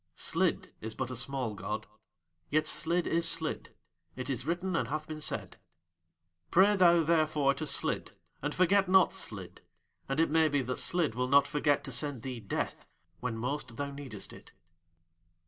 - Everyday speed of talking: Yes, average, 170 wpm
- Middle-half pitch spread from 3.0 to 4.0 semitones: No, average, 4.6 semitones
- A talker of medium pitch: Yes, medium, 145 Hz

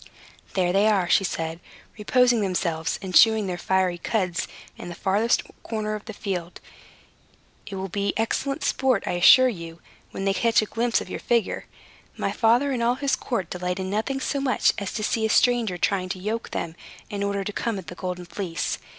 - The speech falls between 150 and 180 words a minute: No, average, 200 wpm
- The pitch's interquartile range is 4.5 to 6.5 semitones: No, average, 4.0 semitones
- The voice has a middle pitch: No, high, 200 Hz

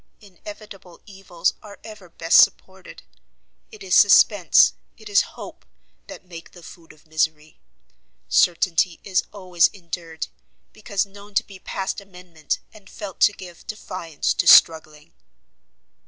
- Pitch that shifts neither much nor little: Yes, average, 3.4 semitones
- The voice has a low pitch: No, medium, 185 Hz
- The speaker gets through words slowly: Yes, slow, 130 wpm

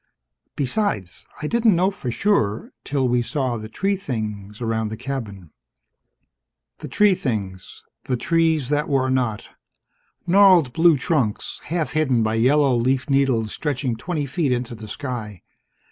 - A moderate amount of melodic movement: No, wide, 5.7 semitones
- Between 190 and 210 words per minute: No, average, 145 wpm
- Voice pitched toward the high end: No, low, 130 Hz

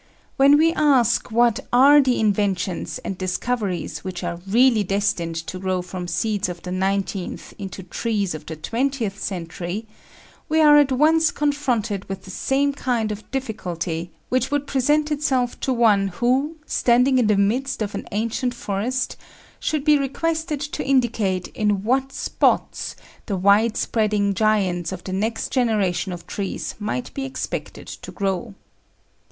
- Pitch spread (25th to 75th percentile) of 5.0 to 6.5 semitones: Yes, wide, 5.6 semitones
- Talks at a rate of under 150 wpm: No, average, 155 wpm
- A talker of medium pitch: No, high, 220 Hz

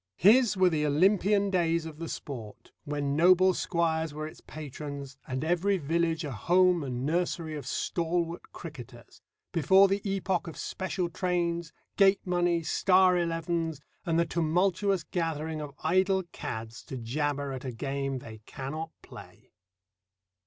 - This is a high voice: No, medium, 165 Hz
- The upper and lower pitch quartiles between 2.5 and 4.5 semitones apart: Yes, average, 3.8 semitones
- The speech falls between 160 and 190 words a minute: No, average, 145 wpm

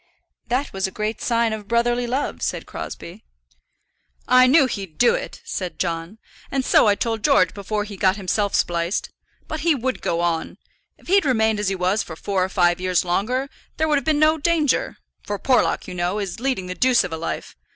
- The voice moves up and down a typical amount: No, wide, 5.8 semitones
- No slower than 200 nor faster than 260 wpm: Yes, fast, 205 wpm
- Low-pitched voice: No, high, 215 Hz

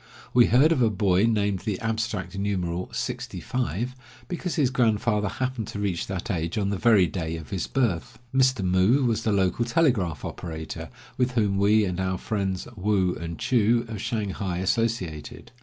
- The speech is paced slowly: No, average, 175 wpm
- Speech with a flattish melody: No, average, 4.2 semitones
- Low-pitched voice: Yes, low, 105 Hz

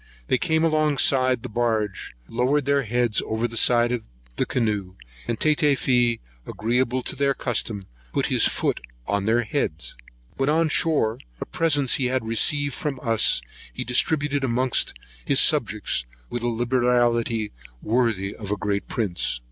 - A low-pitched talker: Yes, low, 120 Hz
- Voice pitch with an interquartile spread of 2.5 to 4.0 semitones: Yes, average, 3.6 semitones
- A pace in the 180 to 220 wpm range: No, average, 150 wpm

